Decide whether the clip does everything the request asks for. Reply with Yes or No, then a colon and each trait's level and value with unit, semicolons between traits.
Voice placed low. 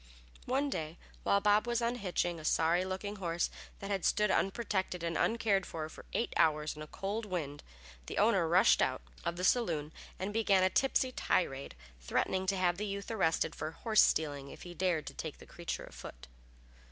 No: medium, 185 Hz